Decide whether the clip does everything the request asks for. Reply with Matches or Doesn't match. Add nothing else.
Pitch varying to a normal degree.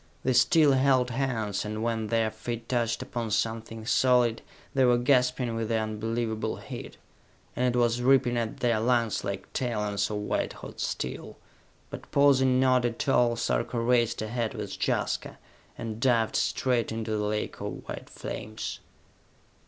Doesn't match